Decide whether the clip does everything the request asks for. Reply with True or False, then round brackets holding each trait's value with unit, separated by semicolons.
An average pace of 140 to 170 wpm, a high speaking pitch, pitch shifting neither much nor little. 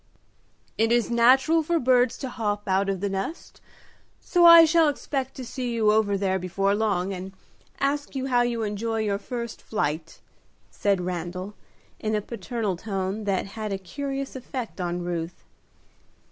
True (160 wpm; 215 Hz; 4.7 semitones)